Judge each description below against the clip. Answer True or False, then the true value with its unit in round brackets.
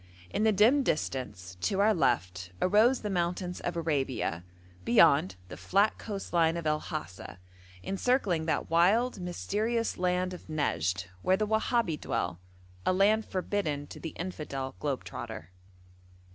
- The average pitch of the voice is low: False (175 Hz)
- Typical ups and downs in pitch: False (7.2 semitones)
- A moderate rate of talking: True (145 wpm)